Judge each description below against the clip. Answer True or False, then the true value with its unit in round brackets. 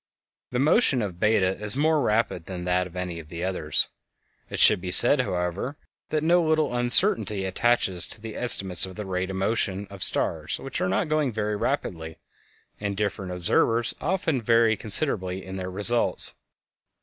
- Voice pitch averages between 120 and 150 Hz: False (105 Hz)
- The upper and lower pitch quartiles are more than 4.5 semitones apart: True (4.9 semitones)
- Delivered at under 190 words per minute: True (175 wpm)